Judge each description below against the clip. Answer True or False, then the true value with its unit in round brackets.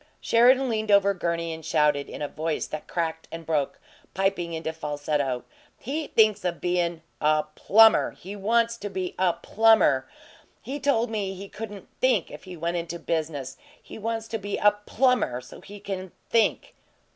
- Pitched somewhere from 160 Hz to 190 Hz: True (185 Hz)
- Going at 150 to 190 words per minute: True (170 wpm)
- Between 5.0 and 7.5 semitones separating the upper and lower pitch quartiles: True (5.3 semitones)